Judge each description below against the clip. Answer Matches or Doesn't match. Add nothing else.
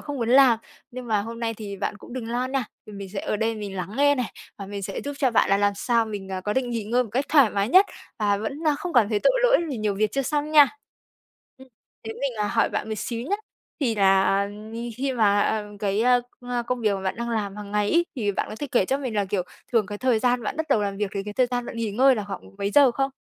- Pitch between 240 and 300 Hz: Doesn't match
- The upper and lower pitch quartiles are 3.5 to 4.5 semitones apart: Matches